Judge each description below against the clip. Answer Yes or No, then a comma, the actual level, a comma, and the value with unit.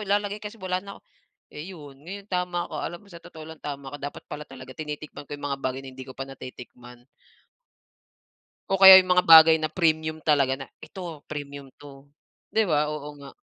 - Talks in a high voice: No, medium, 150 Hz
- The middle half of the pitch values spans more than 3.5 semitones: Yes, average, 4.5 semitones